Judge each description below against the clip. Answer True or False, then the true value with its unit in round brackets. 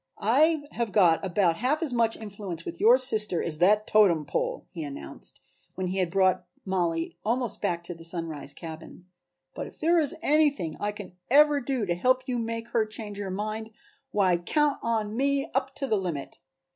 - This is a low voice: False (210 Hz)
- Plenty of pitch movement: True (6.3 semitones)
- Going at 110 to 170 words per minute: False (190 wpm)